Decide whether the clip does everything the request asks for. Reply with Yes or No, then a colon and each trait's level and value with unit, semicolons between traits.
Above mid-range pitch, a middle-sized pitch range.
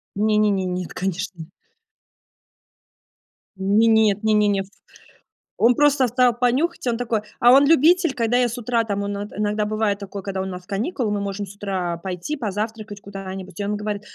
Yes: high, 210 Hz; average, 3.3 semitones